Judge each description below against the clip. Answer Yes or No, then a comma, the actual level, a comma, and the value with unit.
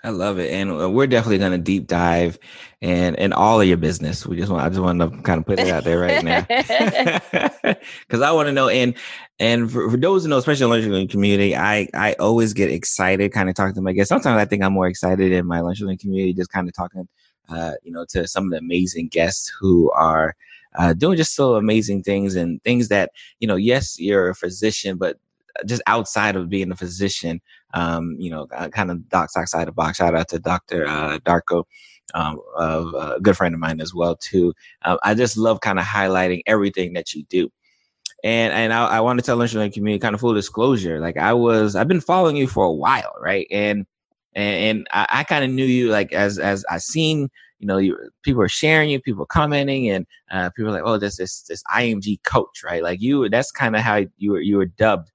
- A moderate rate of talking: No, fast, 230 wpm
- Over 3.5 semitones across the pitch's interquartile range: Yes, average, 4.2 semitones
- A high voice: No, very low, 95 Hz